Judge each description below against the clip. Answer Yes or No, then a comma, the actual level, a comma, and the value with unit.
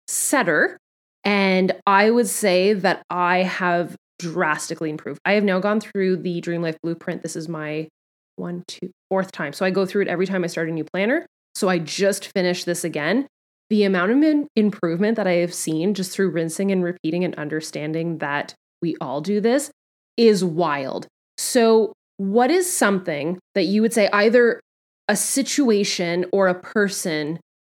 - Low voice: No, medium, 185 Hz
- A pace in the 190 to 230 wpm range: No, average, 175 wpm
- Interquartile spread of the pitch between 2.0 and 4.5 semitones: Yes, average, 3.4 semitones